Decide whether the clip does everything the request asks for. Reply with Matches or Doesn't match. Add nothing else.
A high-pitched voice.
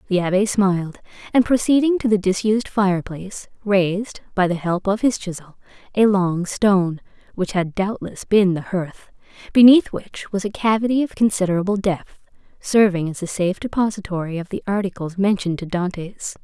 Matches